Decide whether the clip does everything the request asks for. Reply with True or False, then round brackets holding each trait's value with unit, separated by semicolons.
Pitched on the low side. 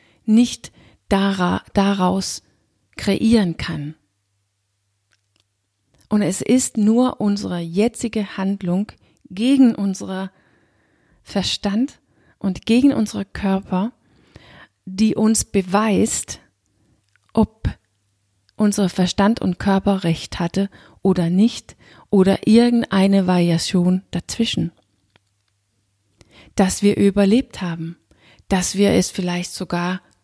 False (190 Hz)